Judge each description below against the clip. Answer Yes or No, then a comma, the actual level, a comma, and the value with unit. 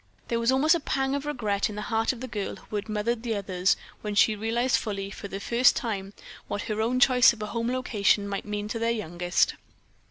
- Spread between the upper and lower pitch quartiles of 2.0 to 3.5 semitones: Yes, average, 3.0 semitones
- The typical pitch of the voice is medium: No, high, 220 Hz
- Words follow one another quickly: Yes, fast, 230 wpm